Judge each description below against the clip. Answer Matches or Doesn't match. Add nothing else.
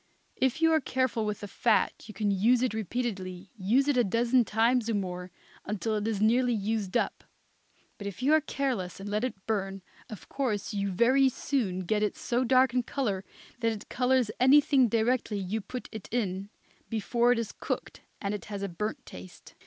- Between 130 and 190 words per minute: Doesn't match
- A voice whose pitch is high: Matches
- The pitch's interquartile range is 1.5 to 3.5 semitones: Doesn't match